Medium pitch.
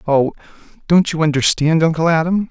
Yes: medium, 160 Hz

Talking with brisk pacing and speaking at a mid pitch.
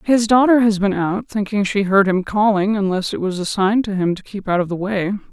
No: fast, 260 wpm; high, 200 Hz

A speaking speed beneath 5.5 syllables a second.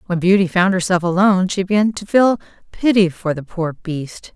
Yes: 5.2 syllables/s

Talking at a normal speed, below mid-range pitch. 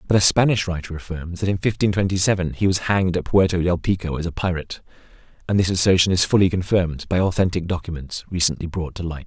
No: fast, 215 wpm; very low, 90 Hz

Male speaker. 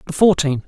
Yes: male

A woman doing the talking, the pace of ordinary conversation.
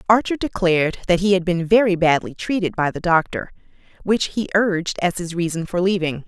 Yes: female; average, 190 wpm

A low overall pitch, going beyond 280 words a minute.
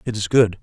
Yes: low, 105 Hz; fast, 290 wpm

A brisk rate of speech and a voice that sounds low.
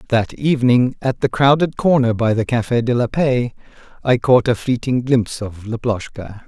No: average, 175 wpm; low, 120 Hz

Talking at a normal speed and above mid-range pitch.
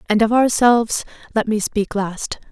Yes: average, 165 wpm; high, 220 Hz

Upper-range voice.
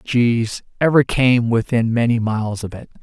No: low, 115 Hz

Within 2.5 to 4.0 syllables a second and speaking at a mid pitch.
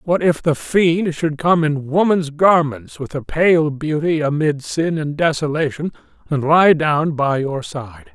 Yes: 3.9 syllables/s; medium, 155 Hz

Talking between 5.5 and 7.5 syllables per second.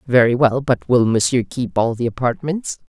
No: 4.9 syllables/s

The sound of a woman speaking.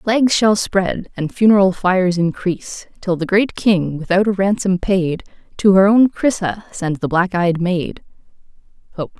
Yes: female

